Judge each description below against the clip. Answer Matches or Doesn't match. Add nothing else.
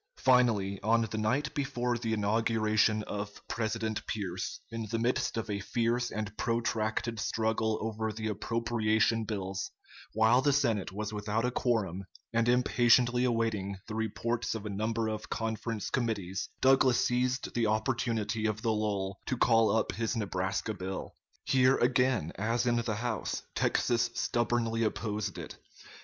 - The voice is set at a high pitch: Doesn't match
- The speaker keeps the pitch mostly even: Matches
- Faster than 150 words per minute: Doesn't match